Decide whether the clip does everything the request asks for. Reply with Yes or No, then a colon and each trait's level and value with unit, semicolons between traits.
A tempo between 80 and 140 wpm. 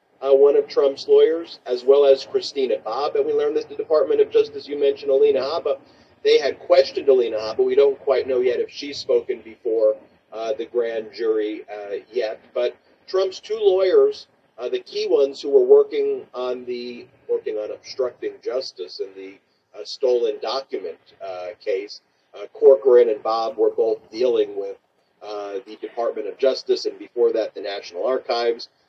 No: average, 175 wpm